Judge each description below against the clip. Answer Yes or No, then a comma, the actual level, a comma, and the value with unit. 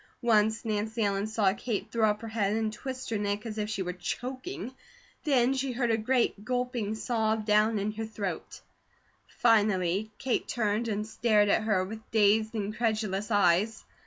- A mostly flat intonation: Yes, narrow, 1.9 semitones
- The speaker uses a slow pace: No, average, 170 wpm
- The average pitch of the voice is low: No, high, 220 Hz